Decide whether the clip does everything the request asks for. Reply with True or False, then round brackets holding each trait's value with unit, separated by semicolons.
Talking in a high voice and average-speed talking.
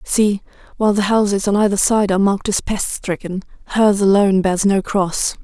True (200 Hz; 190 wpm)